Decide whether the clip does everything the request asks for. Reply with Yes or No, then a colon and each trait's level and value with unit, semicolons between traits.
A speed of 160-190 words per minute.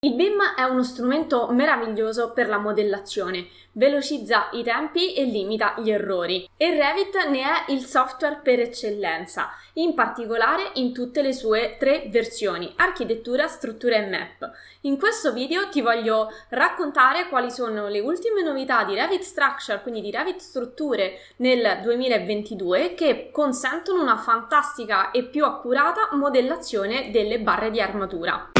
No: average, 145 wpm